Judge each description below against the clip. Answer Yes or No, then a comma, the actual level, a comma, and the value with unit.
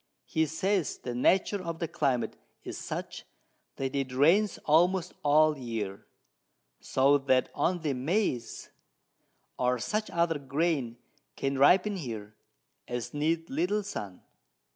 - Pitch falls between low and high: Yes, medium, 150 Hz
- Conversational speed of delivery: No, slow, 125 wpm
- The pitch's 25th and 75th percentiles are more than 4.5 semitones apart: Yes, average, 5.1 semitones